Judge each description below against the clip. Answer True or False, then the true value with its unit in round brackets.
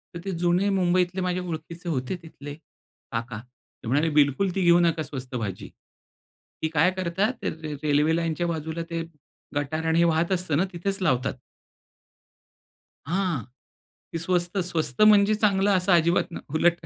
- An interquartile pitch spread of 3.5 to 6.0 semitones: False (3.0 semitones)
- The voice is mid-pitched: True (170 Hz)